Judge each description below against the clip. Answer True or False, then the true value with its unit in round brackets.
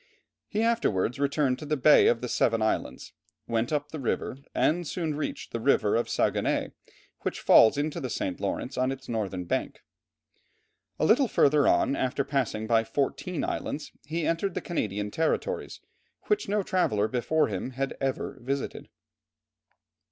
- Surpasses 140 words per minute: True (155 wpm)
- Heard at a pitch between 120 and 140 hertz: True (135 Hz)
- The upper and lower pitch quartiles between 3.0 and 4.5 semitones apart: False (5.4 semitones)